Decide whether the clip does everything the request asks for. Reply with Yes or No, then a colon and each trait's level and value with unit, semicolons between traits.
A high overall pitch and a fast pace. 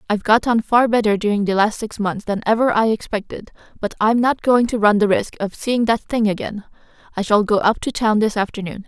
Yes: high, 215 Hz; fast, 235 wpm